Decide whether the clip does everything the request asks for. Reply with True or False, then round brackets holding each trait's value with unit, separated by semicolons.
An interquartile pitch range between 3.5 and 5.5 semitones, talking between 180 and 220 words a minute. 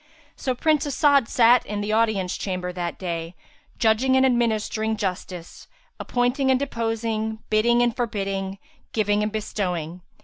False (3.8 semitones; 135 wpm)